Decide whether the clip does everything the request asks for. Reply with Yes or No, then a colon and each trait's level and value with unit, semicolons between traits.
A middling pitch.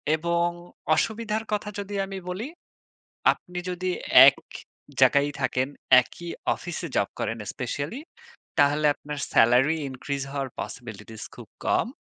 Yes: medium, 150 Hz